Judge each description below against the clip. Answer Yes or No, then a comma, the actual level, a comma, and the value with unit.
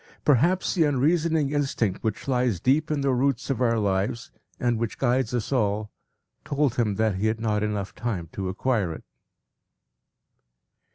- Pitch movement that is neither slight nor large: Yes, average, 4.6 semitones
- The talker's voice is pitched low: Yes, low, 120 Hz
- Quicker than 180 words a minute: No, average, 160 wpm